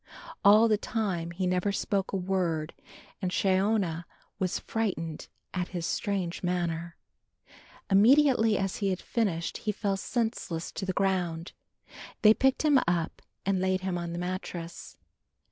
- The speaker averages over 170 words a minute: No, average, 140 wpm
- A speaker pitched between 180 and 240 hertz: Yes, high, 190 Hz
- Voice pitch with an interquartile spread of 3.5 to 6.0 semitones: No, average, 3.1 semitones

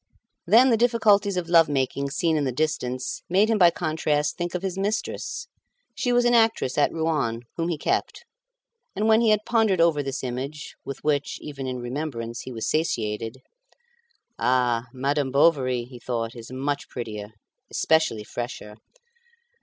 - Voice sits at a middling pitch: Yes, medium, 145 Hz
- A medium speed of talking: Yes, average, 160 wpm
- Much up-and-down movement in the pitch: Yes, wide, 6.2 semitones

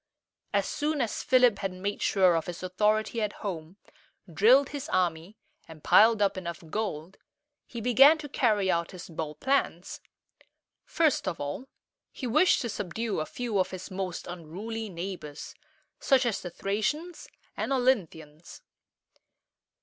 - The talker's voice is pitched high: Yes, high, 200 Hz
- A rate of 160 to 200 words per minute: No, average, 150 wpm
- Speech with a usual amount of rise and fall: No, wide, 5.7 semitones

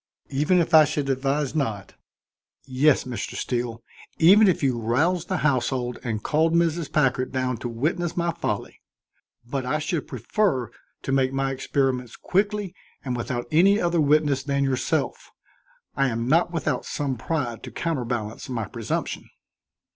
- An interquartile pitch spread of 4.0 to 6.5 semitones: Yes, average, 4.7 semitones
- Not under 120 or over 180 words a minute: Yes, average, 150 wpm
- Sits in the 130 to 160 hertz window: Yes, low, 135 Hz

